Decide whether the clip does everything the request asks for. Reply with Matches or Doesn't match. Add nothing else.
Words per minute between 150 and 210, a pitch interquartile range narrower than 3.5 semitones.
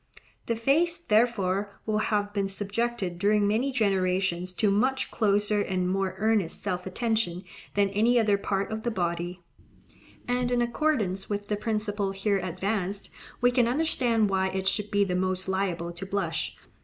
Matches